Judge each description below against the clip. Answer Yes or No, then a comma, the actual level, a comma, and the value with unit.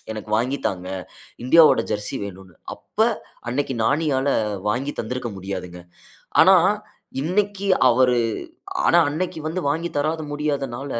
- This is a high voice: No, low, 135 Hz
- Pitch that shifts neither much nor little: No, wide, 6.0 semitones